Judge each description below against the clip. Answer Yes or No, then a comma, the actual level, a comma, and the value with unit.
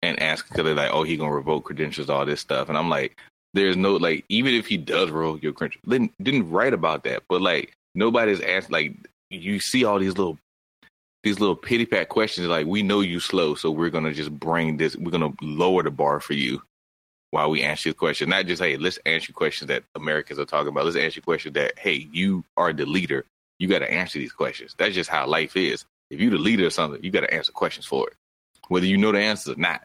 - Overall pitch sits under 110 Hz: Yes, very low, 85 Hz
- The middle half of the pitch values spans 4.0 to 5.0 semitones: Yes, average, 4.5 semitones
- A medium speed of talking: No, fast, 245 wpm